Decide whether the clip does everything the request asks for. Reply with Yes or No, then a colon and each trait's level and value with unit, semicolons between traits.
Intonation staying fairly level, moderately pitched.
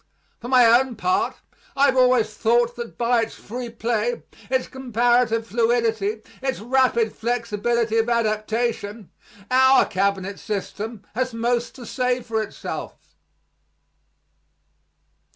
No: narrow, 2.1 semitones; high, 235 Hz